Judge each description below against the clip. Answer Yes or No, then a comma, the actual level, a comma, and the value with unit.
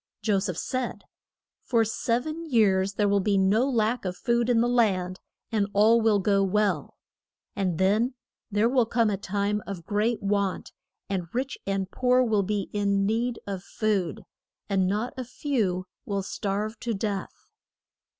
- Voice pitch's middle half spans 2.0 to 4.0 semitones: Yes, average, 3.0 semitones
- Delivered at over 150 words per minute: Yes, average, 165 wpm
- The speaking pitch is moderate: No, high, 210 Hz